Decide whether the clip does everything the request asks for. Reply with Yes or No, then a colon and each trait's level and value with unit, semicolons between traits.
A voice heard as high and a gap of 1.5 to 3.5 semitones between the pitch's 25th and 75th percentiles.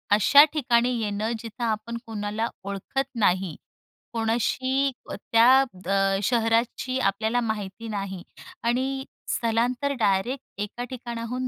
Yes: high, 230 Hz; average, 3.2 semitones